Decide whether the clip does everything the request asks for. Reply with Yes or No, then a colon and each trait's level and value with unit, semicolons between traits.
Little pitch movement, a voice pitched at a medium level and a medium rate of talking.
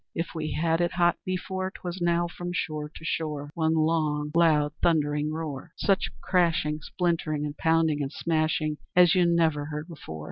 Yes: narrow, 2.2 semitones; medium, 160 Hz; average, 170 wpm